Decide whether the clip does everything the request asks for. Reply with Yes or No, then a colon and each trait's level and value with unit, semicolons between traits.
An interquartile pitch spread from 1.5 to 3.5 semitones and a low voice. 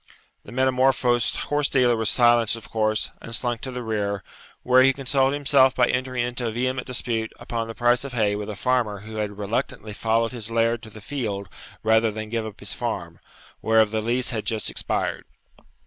Yes: narrow, 2.6 semitones; low, 115 Hz